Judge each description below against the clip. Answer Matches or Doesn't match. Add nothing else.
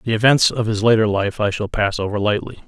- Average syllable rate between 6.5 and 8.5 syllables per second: Doesn't match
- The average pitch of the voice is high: Doesn't match